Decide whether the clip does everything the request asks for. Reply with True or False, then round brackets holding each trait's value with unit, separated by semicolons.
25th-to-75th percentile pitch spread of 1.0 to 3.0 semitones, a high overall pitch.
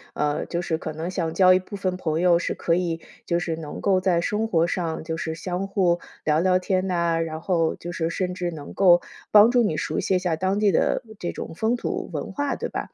False (2.4 semitones; 175 Hz)